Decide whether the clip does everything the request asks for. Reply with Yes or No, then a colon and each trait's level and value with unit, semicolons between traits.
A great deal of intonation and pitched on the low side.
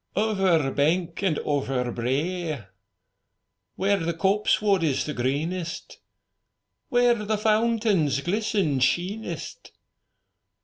No: wide, 6.3 semitones; medium, 175 Hz